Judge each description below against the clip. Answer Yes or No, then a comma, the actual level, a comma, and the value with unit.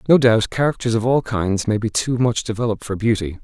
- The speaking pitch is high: No, low, 115 Hz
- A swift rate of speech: Yes, fast, 225 wpm